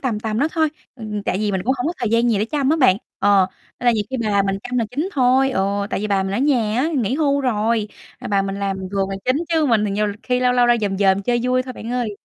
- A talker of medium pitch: No, high, 230 Hz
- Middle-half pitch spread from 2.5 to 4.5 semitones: Yes, average, 4.0 semitones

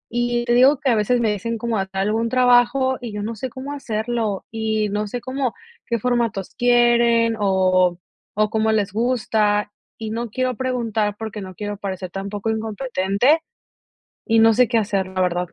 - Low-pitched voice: No, high, 225 Hz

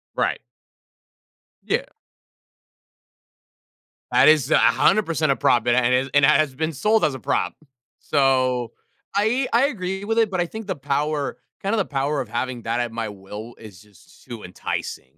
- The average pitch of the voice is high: No, medium, 140 Hz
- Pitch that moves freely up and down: Yes, wide, 7.2 semitones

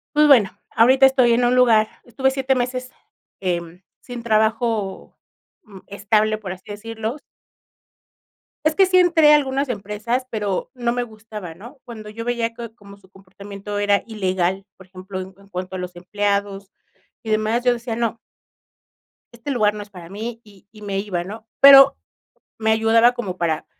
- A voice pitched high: Yes, high, 220 Hz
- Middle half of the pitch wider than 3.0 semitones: Yes, average, 3.5 semitones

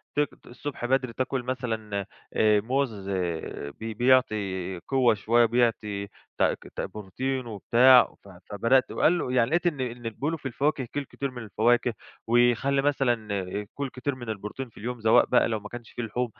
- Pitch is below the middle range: Yes, low, 120 Hz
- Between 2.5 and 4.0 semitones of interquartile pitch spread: Yes, average, 3.4 semitones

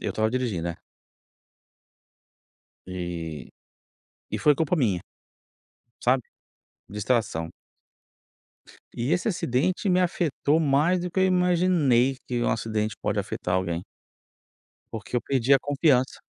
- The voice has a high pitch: No, low, 130 Hz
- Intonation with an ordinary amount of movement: No, wide, 7.3 semitones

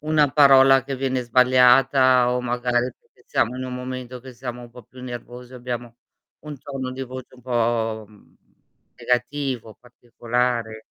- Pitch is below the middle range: Yes, low, 125 Hz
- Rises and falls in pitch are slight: Yes, narrow, 1.2 semitones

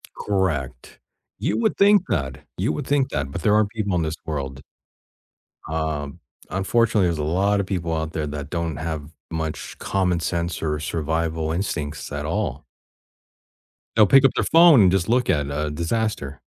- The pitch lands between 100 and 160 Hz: No, very low, 85 Hz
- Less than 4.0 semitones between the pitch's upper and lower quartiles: No, average, 5.1 semitones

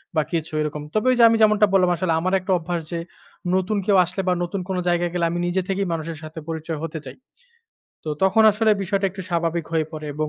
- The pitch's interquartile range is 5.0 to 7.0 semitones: No, average, 3.0 semitones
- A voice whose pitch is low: No, medium, 175 Hz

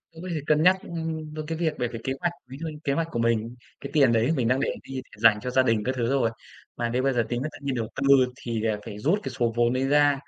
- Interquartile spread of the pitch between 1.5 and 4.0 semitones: No, average, 4.6 semitones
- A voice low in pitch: Yes, low, 130 Hz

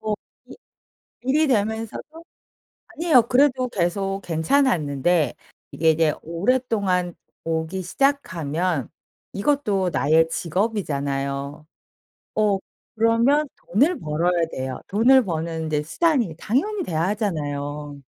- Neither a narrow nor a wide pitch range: No, wide, 7.4 semitones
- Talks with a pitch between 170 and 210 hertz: Yes, medium, 185 Hz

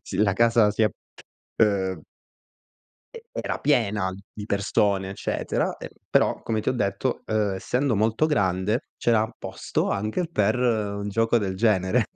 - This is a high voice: No, low, 105 Hz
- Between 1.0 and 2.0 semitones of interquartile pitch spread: No, average, 2.7 semitones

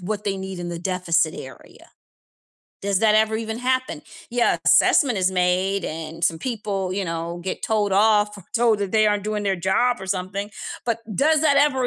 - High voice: Yes, high, 200 Hz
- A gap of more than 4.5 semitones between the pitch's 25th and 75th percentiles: No, average, 3.3 semitones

